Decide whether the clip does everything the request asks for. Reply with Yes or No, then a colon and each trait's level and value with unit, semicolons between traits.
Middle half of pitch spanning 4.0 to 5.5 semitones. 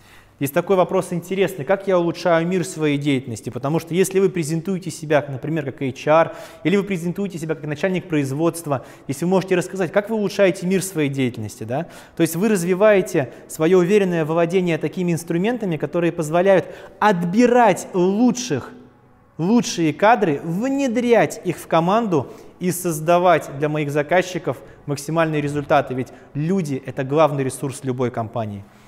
Yes: average, 4.5 semitones